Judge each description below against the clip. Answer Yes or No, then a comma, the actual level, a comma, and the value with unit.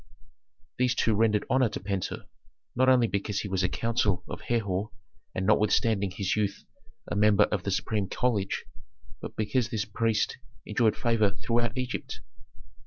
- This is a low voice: Yes, low, 110 Hz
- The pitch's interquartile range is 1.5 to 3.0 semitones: Yes, average, 2.7 semitones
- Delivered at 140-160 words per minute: Yes, average, 155 wpm